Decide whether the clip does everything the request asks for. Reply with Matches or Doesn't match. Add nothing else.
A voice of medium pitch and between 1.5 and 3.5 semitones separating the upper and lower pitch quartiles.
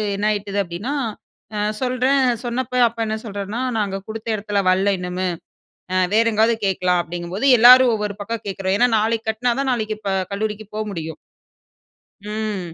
Doesn't match